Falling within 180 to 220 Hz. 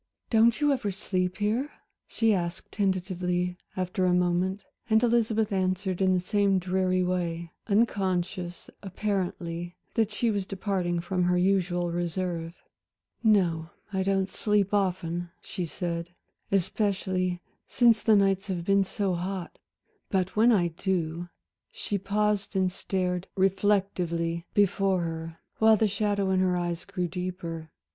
Yes: medium, 185 Hz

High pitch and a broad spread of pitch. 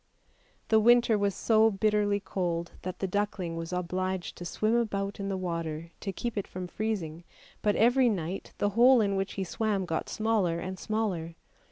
No: high, 195 Hz; average, 3.4 semitones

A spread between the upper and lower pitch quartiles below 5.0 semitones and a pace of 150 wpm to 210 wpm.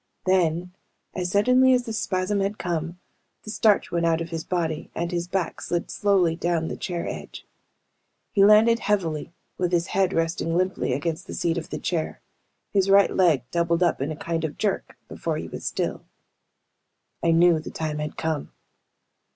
Yes: average, 2.9 semitones; average, 180 wpm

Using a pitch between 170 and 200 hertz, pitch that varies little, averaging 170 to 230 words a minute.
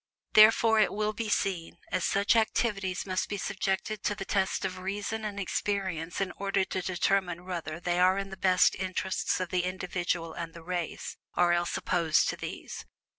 Yes: medium, 185 Hz; narrow, 2.1 semitones; average, 180 wpm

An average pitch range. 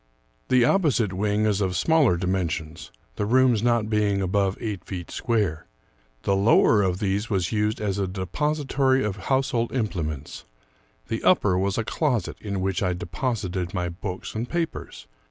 Yes: average, 4.1 semitones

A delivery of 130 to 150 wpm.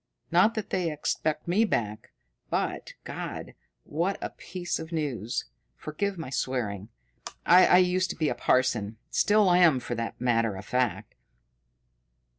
Yes: average, 140 wpm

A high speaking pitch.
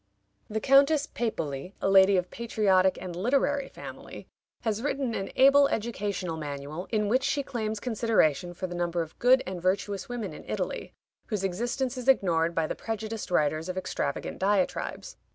Yes: high, 205 Hz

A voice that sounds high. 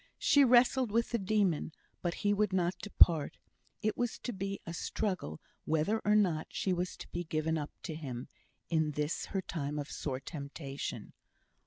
No: medium, 175 Hz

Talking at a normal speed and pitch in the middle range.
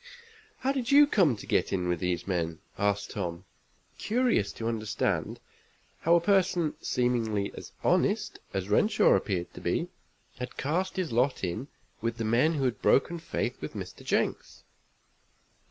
No: average, 155 wpm; low, 120 Hz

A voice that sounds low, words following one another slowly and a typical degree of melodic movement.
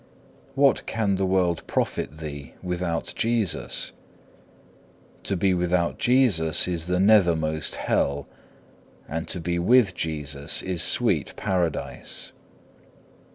Yes: very low, 90 Hz; slow, 110 wpm; average, 3.1 semitones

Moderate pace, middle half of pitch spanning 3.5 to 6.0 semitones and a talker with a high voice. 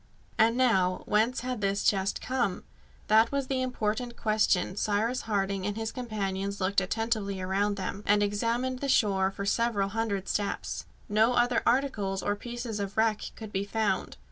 No: average, 165 wpm; average, 3.0 semitones; high, 210 Hz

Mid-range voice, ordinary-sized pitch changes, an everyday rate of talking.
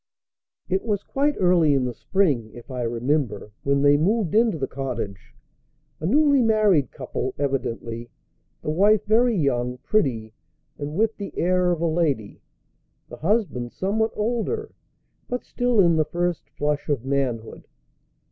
No: medium, 155 Hz; wide, 8.5 semitones; average, 145 wpm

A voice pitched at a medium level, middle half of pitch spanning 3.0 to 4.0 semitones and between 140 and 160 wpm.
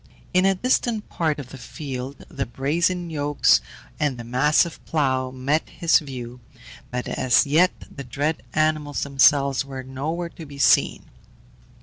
Yes: medium, 145 Hz; average, 3.4 semitones; average, 145 wpm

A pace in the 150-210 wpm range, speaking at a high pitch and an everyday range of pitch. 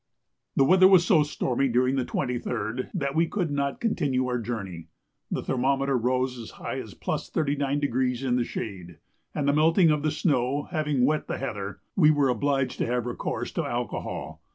No: average, 175 wpm; low, 135 Hz; average, 3.3 semitones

